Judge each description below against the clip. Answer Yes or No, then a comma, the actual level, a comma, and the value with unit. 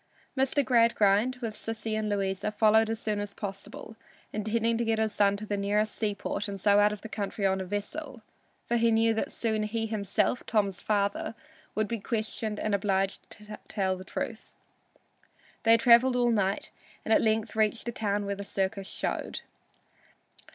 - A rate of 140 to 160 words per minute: No, average, 180 wpm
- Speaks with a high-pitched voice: Yes, high, 215 Hz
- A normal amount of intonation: No, narrow, 1.9 semitones